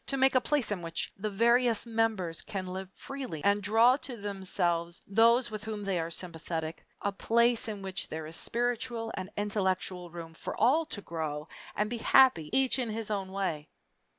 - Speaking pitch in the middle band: No, high, 205 Hz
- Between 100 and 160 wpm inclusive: No, average, 185 wpm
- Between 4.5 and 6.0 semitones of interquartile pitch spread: Yes, average, 4.8 semitones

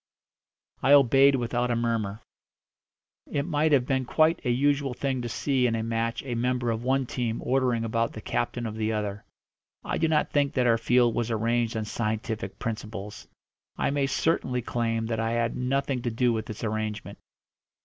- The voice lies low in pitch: Yes, low, 120 Hz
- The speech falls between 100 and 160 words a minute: No, average, 185 wpm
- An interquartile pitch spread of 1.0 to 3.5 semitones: Yes, average, 2.8 semitones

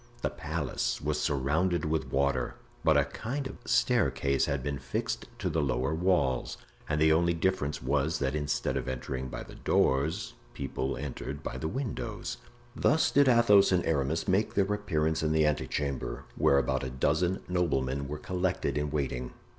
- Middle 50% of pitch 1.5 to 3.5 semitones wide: No, average, 4.6 semitones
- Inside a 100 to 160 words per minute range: No, average, 170 wpm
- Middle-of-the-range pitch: No, very low, 75 Hz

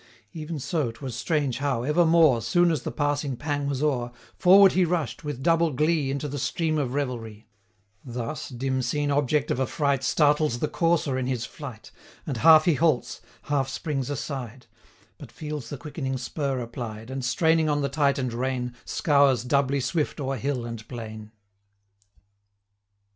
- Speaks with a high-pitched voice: No, medium, 140 Hz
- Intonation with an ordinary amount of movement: Yes, average, 3.3 semitones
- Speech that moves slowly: No, average, 165 wpm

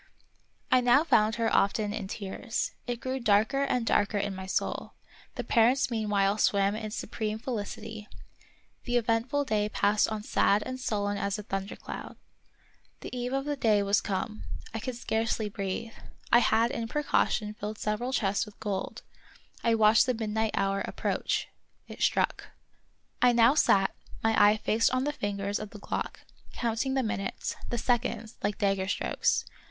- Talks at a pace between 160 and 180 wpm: Yes, average, 165 wpm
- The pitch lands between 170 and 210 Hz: No, high, 220 Hz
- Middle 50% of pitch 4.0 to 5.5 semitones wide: No, average, 2.7 semitones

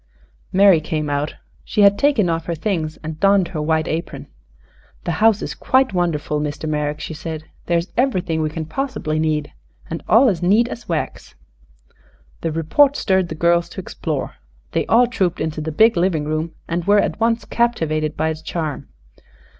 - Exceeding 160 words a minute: Yes, average, 180 wpm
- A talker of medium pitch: Yes, medium, 170 Hz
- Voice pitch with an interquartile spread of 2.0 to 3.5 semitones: No, average, 4.4 semitones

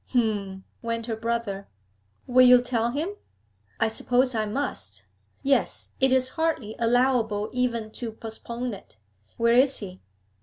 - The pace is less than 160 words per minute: Yes, average, 140 wpm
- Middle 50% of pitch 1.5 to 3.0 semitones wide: Yes, narrow, 2.6 semitones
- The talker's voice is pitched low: No, high, 235 Hz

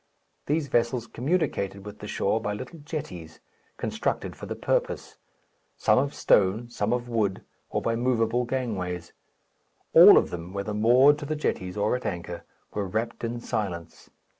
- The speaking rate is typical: Yes, average, 160 wpm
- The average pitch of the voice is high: No, low, 115 Hz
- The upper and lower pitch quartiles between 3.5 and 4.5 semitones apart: Yes, average, 4.2 semitones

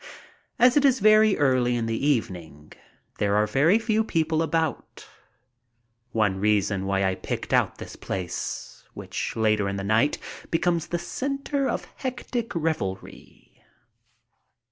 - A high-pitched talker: No, medium, 140 Hz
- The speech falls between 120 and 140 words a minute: Yes, slow, 135 wpm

